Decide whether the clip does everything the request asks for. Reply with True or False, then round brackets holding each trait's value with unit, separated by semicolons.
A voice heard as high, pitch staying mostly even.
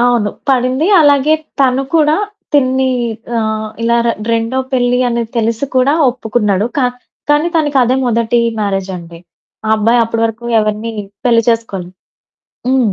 False (235 Hz; 3.2 semitones)